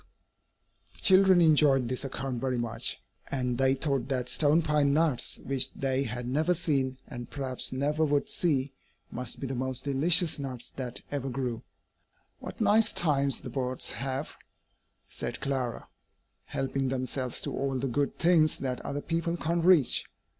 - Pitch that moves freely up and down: No, average, 2.9 semitones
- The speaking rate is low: No, average, 160 wpm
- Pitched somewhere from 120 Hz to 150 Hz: Yes, low, 135 Hz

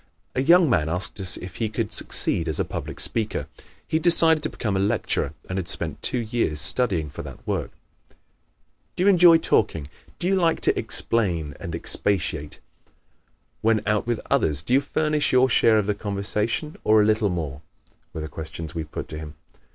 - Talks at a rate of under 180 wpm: No, average, 190 wpm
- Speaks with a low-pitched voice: Yes, low, 105 Hz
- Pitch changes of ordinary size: No, wide, 7.5 semitones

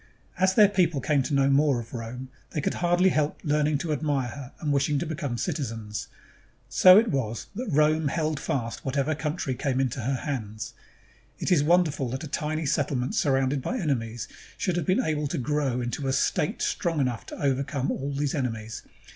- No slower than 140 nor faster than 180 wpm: No, average, 190 wpm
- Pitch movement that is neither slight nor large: Yes, average, 3.2 semitones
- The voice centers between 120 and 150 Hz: Yes, medium, 140 Hz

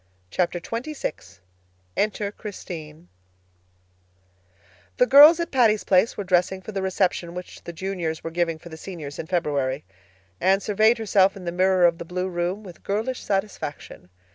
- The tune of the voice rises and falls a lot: No, average, 3.4 semitones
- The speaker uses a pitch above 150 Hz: Yes, medium, 185 Hz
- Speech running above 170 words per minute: No, average, 155 wpm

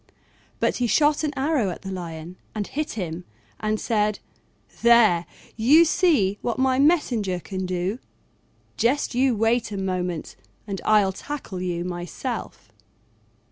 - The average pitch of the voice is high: Yes, high, 215 Hz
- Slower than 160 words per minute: Yes, average, 140 wpm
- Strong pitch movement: Yes, wide, 5.9 semitones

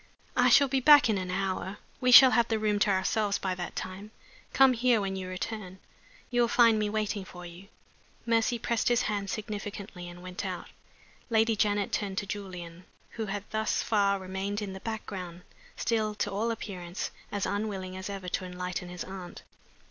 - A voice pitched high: Yes, high, 205 Hz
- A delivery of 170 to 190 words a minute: Yes, average, 185 wpm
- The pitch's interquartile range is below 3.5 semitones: Yes, average, 3.0 semitones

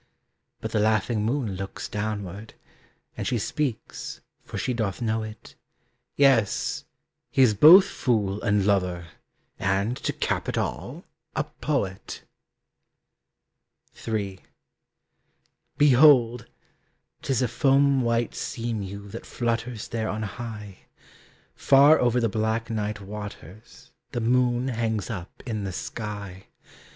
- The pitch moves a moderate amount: Yes, average, 3.2 semitones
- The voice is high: No, low, 110 Hz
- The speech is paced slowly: Yes, slow, 120 wpm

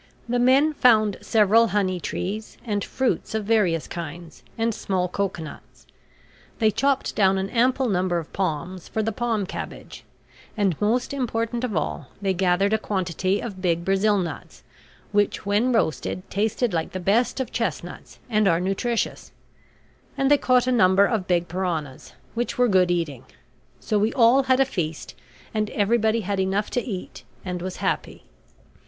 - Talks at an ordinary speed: Yes, average, 160 wpm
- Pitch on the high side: Yes, high, 205 Hz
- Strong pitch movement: No, average, 4.1 semitones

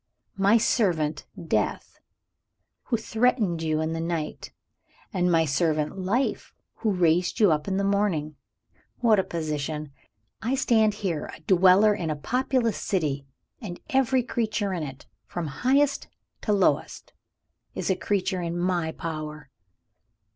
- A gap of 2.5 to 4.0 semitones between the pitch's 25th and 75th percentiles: No, average, 5.2 semitones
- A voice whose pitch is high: No, medium, 180 Hz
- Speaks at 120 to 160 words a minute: Yes, average, 140 wpm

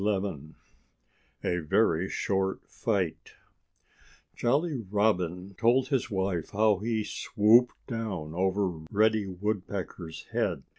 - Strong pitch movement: No, average, 3.3 semitones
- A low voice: Yes, low, 100 Hz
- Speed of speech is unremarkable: No, slow, 100 wpm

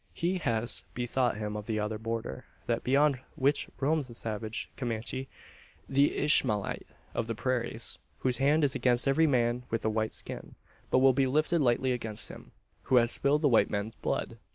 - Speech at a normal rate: Yes, average, 180 wpm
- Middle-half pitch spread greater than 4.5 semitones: No, average, 3.4 semitones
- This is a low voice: Yes, low, 125 Hz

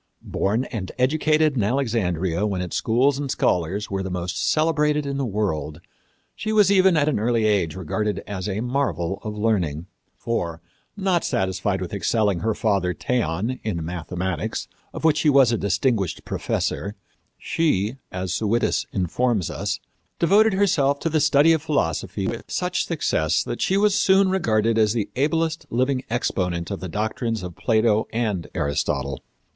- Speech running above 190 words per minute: No, average, 160 wpm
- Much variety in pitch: Yes, wide, 7.2 semitones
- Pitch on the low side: Yes, low, 110 Hz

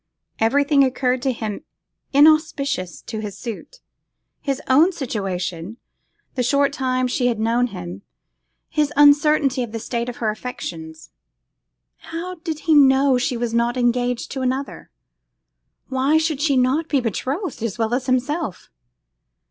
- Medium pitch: No, very high, 255 Hz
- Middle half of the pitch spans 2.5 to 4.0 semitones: Yes, average, 3.7 semitones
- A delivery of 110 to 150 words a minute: Yes, average, 140 wpm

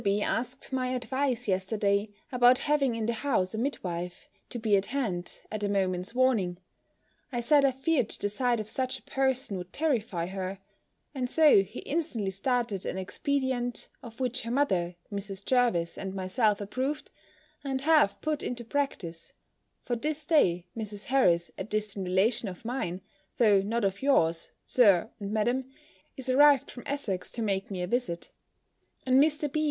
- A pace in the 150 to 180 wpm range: Yes, average, 170 wpm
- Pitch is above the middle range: Yes, high, 230 Hz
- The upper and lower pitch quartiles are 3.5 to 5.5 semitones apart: Yes, average, 5.2 semitones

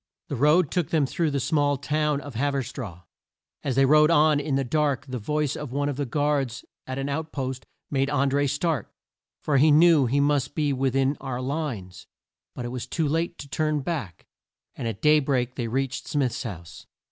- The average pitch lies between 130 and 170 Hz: Yes, medium, 140 Hz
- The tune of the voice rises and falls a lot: No, average, 2.7 semitones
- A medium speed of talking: No, fast, 210 wpm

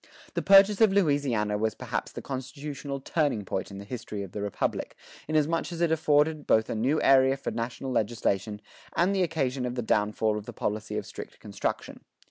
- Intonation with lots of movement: Yes, wide, 6.3 semitones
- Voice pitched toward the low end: Yes, low, 130 Hz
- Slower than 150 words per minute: No, average, 190 wpm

